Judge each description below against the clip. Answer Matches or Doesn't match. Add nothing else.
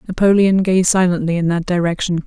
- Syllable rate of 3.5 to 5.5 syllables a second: Doesn't match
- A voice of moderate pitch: Matches